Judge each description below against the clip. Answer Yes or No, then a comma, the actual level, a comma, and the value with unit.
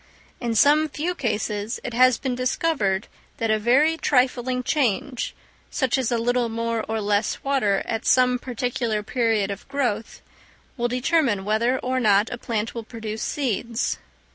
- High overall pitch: Yes, high, 240 Hz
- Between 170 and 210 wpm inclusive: No, average, 155 wpm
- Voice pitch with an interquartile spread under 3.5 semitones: Yes, average, 2.8 semitones